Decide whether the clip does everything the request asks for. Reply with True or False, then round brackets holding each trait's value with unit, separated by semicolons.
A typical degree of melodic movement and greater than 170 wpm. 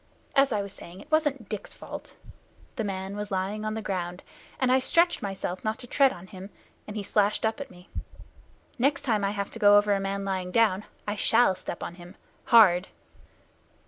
True (3.0 semitones; 205 wpm)